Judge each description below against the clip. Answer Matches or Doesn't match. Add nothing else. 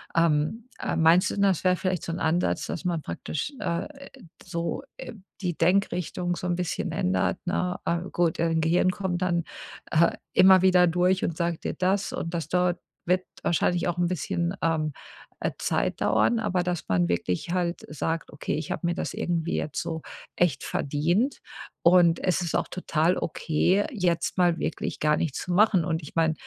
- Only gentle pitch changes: Matches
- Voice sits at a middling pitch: Matches